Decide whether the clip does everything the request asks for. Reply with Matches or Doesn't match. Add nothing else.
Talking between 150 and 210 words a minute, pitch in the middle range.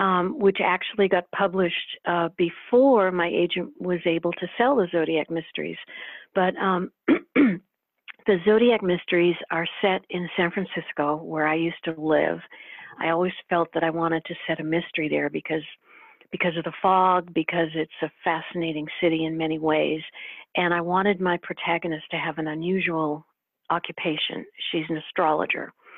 Matches